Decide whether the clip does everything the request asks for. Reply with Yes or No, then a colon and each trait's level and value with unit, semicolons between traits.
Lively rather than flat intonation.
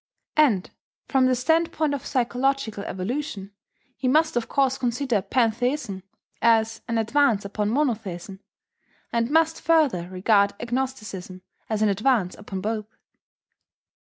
No: average, 4.8 semitones